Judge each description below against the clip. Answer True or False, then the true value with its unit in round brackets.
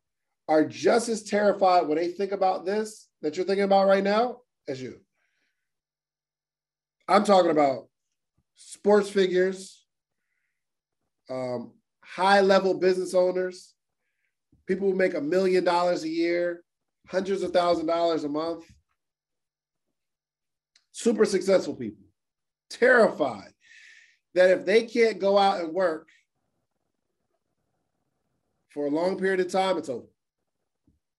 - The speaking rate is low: True (115 wpm)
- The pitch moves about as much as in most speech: False (2.3 semitones)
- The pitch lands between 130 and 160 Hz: False (185 Hz)